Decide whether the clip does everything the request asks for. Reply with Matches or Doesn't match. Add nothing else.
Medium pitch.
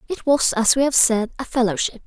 Doesn't match